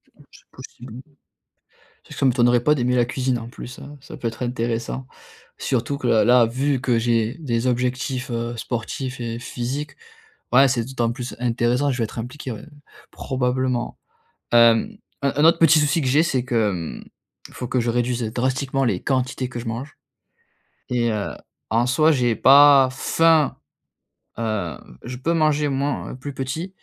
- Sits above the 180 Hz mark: No, low, 125 Hz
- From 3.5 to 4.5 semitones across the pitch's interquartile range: No, narrow, 2.6 semitones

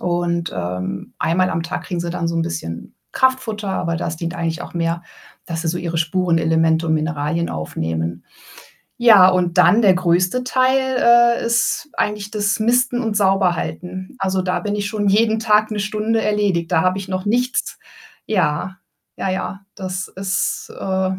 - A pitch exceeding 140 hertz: Yes, medium, 185 Hz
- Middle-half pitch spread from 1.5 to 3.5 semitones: No, average, 4.1 semitones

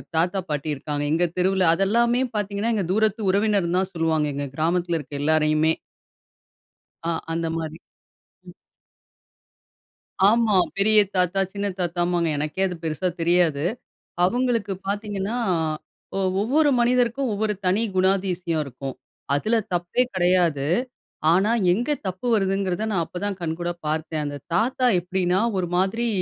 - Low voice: No, medium, 185 Hz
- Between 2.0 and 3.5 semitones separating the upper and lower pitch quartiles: No, average, 4.1 semitones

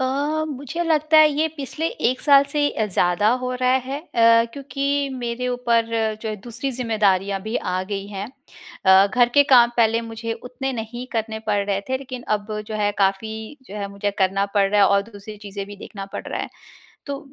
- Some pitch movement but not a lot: Yes, average, 4.1 semitones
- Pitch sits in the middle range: No, high, 230 Hz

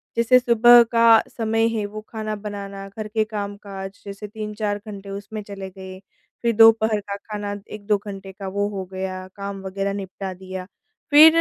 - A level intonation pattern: Yes, narrow, 1.8 semitones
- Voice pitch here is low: No, high, 205 Hz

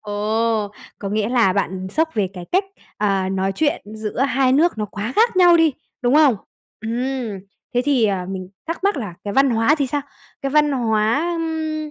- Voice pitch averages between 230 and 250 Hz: Yes, high, 240 Hz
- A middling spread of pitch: No, wide, 6.4 semitones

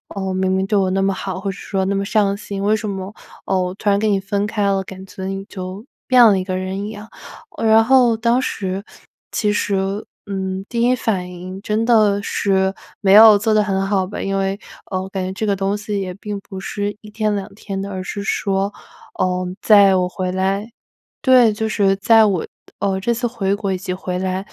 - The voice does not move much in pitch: Yes, narrow, 1.8 semitones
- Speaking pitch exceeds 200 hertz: No, high, 195 Hz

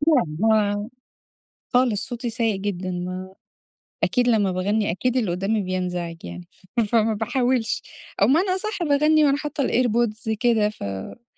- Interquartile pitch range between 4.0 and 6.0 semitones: Yes, average, 4.9 semitones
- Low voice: No, high, 220 Hz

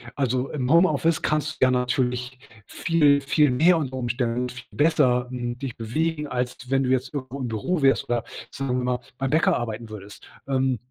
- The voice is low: Yes, low, 130 Hz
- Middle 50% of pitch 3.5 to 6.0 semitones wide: No, average, 2.8 semitones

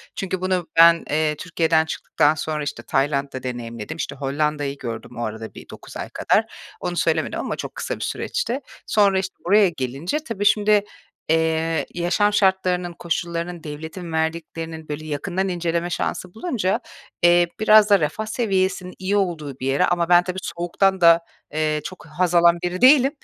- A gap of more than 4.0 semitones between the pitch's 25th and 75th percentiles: No, average, 3.6 semitones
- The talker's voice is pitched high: No, medium, 170 Hz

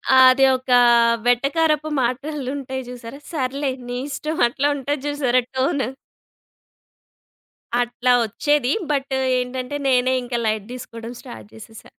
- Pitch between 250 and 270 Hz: Yes, very high, 260 Hz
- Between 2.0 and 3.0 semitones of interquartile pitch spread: Yes, narrow, 2.4 semitones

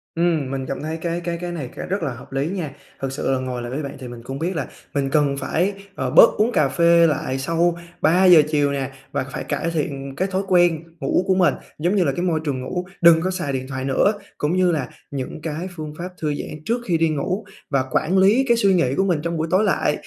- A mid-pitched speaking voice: Yes, medium, 160 Hz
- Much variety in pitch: No, average, 4.4 semitones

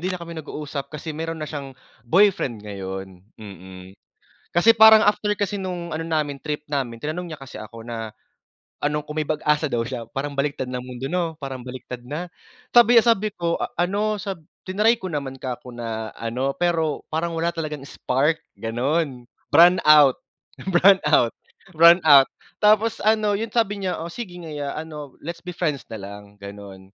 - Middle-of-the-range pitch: Yes, medium, 150 Hz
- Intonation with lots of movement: Yes, wide, 5.9 semitones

